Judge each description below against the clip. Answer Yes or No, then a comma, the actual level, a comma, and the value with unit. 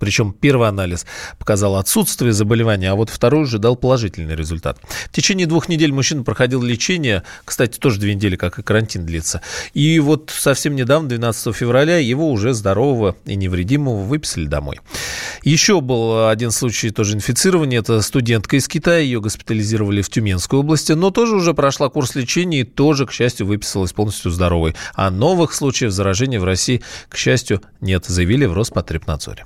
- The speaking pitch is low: Yes, low, 120 Hz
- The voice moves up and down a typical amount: No, wide, 5.9 semitones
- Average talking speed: No, fast, 165 wpm